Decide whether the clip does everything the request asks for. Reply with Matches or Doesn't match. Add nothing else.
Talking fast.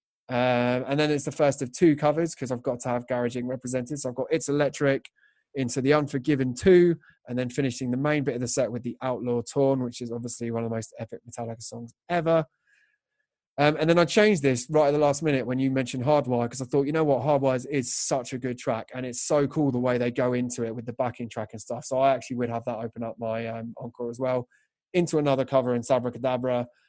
Matches